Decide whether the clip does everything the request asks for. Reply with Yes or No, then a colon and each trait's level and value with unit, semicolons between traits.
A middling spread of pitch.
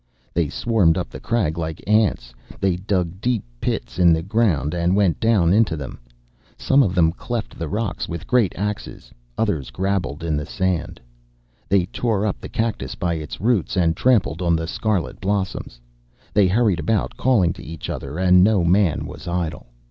Yes: average, 4.2 semitones